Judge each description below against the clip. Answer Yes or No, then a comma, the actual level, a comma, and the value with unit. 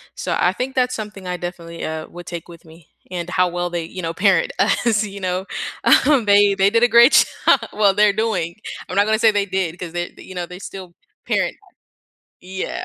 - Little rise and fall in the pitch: No, average, 3.0 semitones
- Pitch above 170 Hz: Yes, medium, 185 Hz